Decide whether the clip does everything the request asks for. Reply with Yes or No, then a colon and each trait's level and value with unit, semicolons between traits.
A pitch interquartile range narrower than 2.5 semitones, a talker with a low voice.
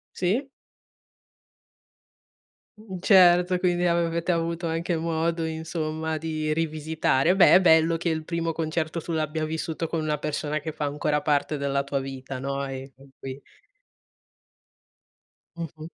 No: narrow, 2.0 semitones; medium, 160 Hz